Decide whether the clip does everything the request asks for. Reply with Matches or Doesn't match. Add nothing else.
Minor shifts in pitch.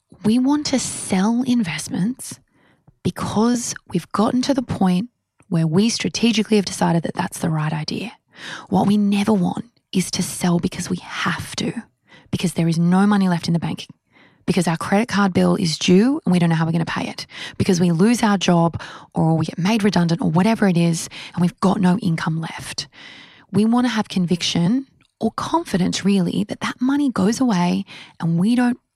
Doesn't match